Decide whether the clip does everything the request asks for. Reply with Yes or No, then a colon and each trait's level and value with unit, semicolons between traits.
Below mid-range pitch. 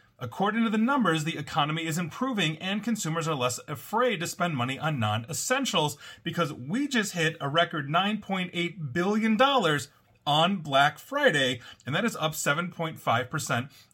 No: medium, 170 Hz